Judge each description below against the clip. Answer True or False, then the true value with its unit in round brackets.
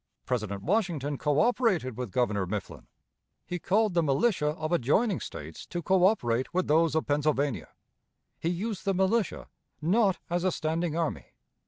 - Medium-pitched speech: True (165 Hz)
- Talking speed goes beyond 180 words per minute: False (145 wpm)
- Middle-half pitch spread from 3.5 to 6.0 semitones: True (5.1 semitones)